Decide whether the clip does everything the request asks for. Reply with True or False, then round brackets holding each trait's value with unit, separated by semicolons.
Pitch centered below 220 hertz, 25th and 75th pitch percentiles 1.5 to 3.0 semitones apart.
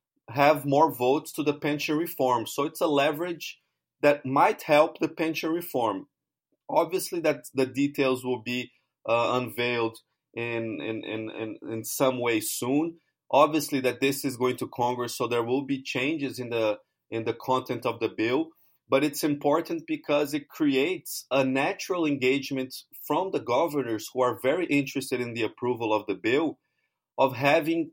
False (135 Hz; 3.7 semitones)